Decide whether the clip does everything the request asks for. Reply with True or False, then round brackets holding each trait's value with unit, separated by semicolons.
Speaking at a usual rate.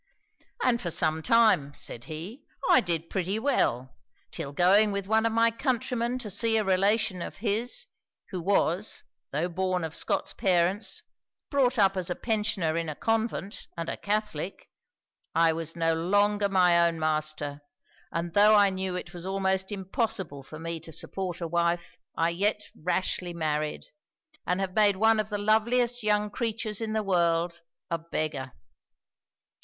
True (165 wpm)